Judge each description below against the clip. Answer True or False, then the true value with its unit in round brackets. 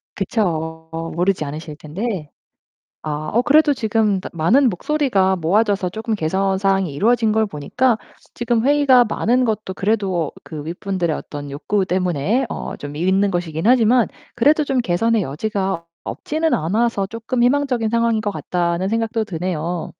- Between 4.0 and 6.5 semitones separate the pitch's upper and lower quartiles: True (5.3 semitones)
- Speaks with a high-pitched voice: True (200 Hz)